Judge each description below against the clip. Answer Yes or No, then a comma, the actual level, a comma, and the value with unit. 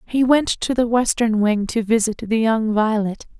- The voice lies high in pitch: Yes, high, 225 Hz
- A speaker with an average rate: Yes, average, 195 wpm